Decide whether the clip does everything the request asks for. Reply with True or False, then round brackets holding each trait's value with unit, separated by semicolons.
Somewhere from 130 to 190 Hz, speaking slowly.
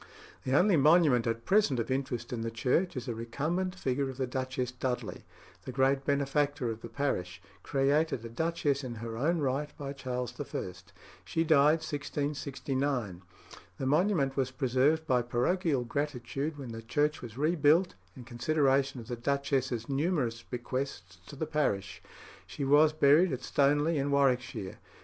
False (135 Hz; 160 wpm)